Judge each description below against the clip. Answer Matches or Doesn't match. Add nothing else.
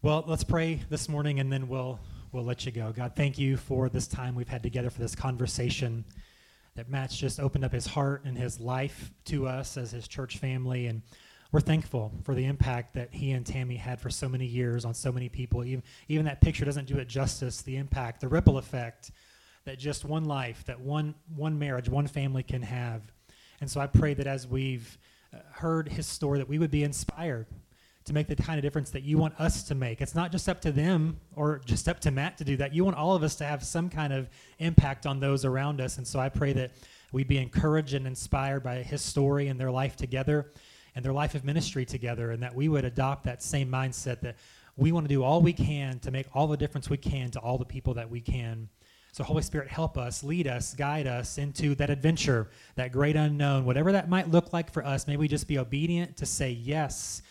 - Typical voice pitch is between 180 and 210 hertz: Doesn't match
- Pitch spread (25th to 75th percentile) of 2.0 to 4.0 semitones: Matches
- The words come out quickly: Matches